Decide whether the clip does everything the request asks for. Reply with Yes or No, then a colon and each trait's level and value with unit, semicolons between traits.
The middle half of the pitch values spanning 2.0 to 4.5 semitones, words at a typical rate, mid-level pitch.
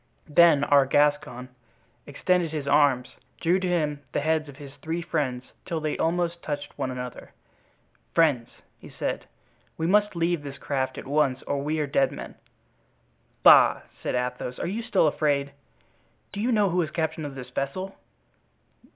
Yes: average, 3.6 semitones; average, 165 wpm; medium, 150 Hz